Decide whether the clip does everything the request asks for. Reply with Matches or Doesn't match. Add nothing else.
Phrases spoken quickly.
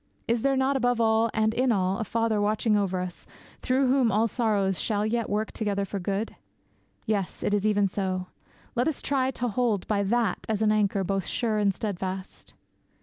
Doesn't match